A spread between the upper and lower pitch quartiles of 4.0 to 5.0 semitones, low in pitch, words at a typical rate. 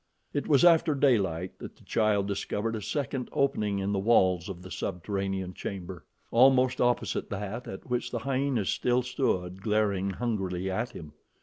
Yes: average, 4.6 semitones; low, 105 Hz; average, 165 wpm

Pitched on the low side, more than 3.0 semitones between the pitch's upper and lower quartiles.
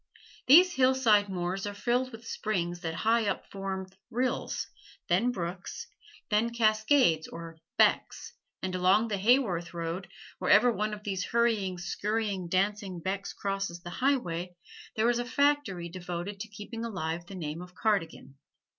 No: high, 200 Hz; average, 4.5 semitones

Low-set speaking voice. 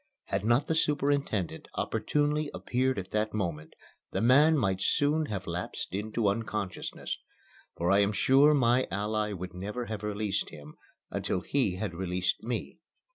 Yes: low, 105 Hz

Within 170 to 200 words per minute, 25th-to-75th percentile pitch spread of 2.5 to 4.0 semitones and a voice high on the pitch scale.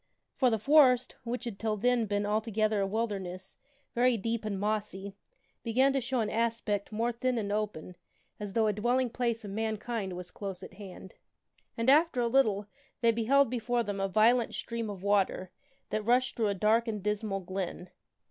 Yes: average, 185 wpm; average, 2.8 semitones; high, 220 Hz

